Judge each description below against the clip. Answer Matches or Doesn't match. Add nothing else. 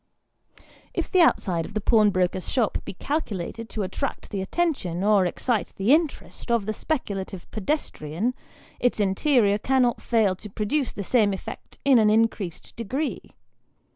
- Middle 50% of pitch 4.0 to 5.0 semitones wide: Matches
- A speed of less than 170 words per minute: Matches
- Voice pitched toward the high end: Matches